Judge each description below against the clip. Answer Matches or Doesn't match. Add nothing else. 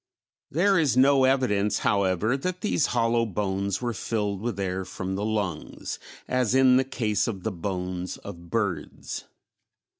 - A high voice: Doesn't match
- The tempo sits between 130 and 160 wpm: Matches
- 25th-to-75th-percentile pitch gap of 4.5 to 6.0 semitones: Matches